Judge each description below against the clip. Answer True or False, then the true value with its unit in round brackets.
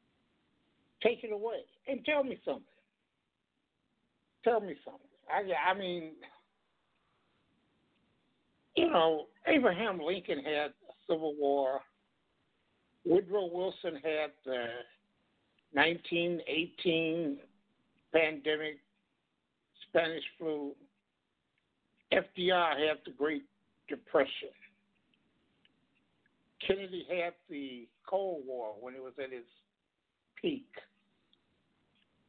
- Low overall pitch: False (170 Hz)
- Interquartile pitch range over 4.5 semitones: True (4.9 semitones)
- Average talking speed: False (85 wpm)